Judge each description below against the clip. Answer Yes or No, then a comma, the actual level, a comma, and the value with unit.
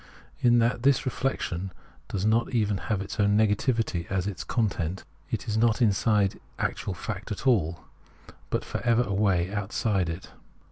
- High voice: No, low, 105 Hz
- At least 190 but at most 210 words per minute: No, average, 160 wpm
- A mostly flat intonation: No, average, 3.2 semitones